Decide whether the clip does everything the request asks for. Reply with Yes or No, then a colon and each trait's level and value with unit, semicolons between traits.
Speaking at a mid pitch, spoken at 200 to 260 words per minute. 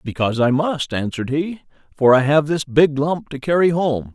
Yes: medium, 145 Hz; fast, 205 wpm